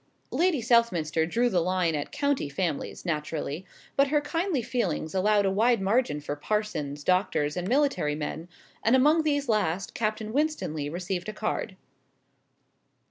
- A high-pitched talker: Yes, high, 195 Hz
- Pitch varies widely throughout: Yes, wide, 7.4 semitones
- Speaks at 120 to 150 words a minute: Yes, average, 145 wpm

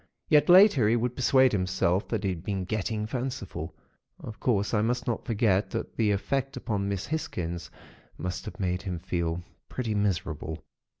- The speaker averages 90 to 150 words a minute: No, average, 170 wpm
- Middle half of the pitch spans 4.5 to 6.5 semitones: Yes, average, 4.9 semitones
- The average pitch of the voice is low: Yes, low, 105 Hz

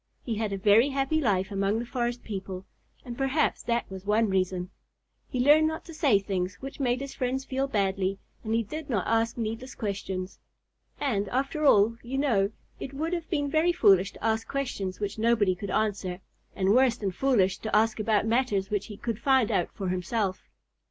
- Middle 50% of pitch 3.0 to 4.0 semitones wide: No, average, 5.1 semitones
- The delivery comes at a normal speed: Yes, average, 195 wpm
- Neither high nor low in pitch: No, high, 225 Hz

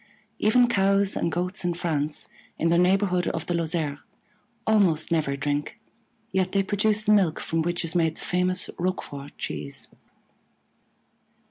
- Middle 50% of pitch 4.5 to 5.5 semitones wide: No, average, 3.5 semitones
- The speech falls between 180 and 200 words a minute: No, average, 145 wpm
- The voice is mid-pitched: Yes, medium, 175 Hz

